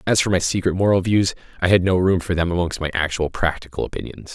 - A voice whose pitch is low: Yes, very low, 90 Hz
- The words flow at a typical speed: No, fast, 235 wpm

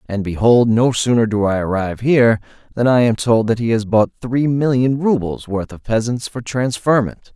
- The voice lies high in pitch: No, low, 115 Hz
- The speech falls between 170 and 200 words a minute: Yes, average, 195 wpm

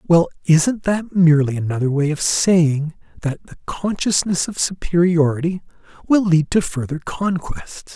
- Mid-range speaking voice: Yes, medium, 170 Hz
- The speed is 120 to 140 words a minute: Yes, slow, 135 wpm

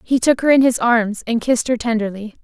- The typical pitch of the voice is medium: No, high, 235 Hz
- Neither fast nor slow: No, fast, 245 wpm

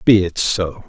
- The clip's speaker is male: Yes, male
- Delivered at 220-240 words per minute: No, fast, 205 wpm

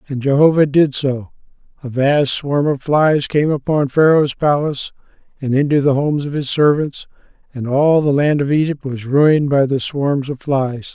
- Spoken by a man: Yes, male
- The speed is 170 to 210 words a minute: Yes, average, 180 wpm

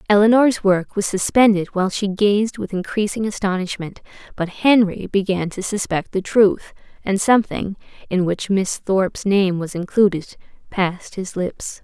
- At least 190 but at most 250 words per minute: No, average, 145 wpm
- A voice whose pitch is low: No, high, 195 Hz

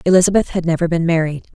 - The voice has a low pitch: No, medium, 170 Hz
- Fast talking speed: No, average, 190 wpm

